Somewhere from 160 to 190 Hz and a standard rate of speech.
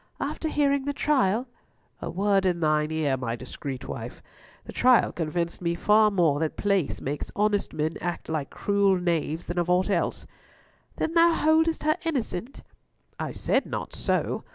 Yes: medium, 185 Hz; average, 165 wpm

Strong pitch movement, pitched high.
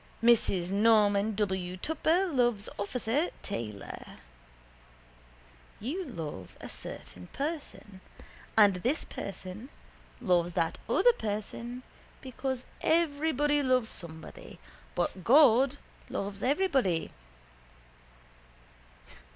Yes: wide, 6.6 semitones; high, 225 Hz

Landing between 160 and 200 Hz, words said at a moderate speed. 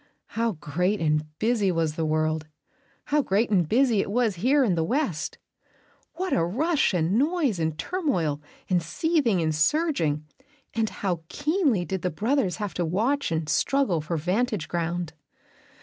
Yes: high, 190 Hz; average, 160 wpm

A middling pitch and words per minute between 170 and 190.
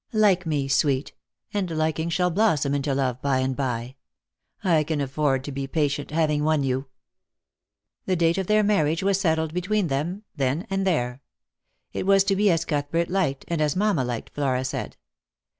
Yes: medium, 155 Hz; average, 175 wpm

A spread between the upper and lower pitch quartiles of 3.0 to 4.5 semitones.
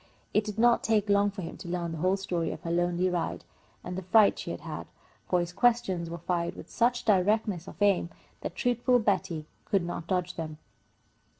Yes: average, 3.5 semitones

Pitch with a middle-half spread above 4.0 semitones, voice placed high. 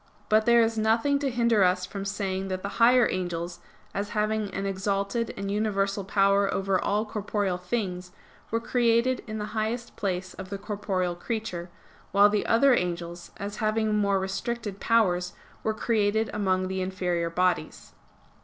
No: average, 2.8 semitones; high, 200 Hz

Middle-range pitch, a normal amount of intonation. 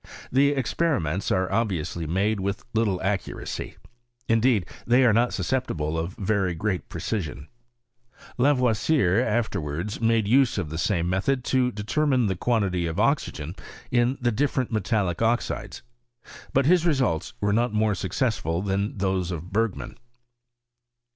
No: low, 105 Hz; average, 4.9 semitones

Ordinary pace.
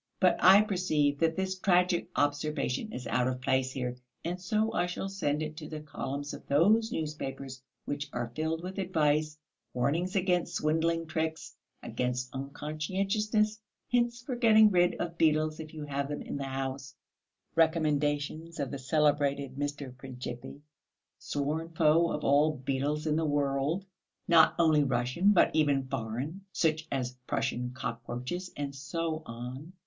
Yes: average, 150 wpm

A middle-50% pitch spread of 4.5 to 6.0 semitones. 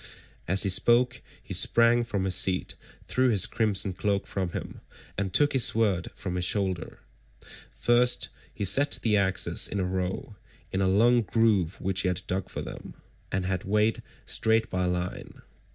No: average, 3.5 semitones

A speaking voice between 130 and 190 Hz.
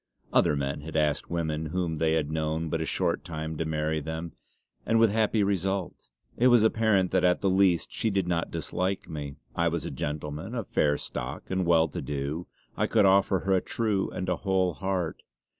No: very low, 85 Hz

